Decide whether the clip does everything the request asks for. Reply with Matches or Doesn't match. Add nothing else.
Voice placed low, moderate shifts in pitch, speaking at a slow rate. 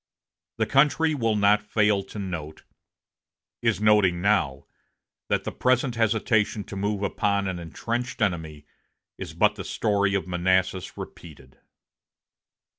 Matches